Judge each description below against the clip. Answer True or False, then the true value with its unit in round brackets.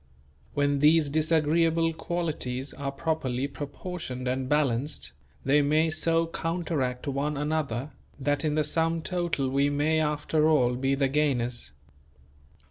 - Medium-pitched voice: True (150 Hz)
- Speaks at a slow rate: True (130 wpm)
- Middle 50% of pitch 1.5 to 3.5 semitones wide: True (2.6 semitones)